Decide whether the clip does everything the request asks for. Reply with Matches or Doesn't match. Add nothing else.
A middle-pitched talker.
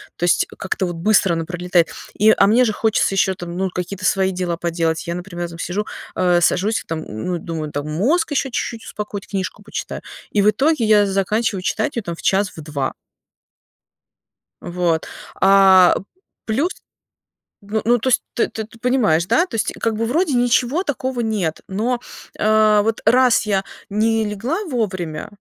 Doesn't match